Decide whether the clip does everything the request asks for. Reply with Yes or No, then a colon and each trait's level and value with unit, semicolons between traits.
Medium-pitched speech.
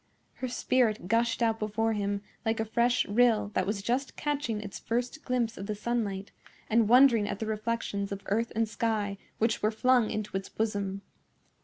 No: high, 220 Hz